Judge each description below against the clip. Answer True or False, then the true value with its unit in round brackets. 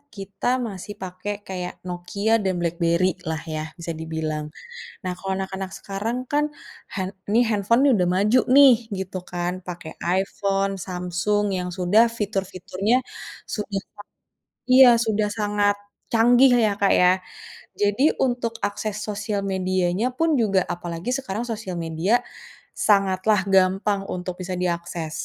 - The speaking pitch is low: False (195 Hz)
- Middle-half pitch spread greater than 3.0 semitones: False (2.7 semitones)